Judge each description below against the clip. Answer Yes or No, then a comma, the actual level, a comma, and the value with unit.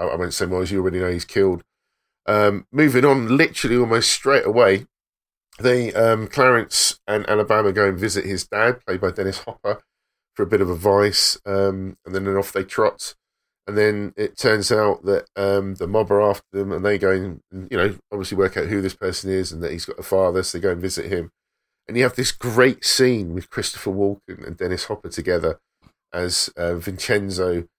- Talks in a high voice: No, low, 100 Hz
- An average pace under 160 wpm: No, fast, 205 wpm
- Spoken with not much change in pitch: Yes, narrow, 2.0 semitones